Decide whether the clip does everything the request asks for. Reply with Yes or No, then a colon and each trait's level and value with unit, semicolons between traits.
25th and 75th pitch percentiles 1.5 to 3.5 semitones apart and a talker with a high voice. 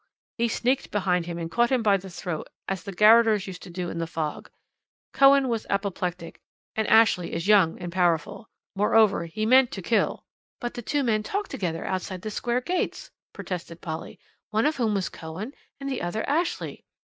No: average, 5.0 semitones; high, 205 Hz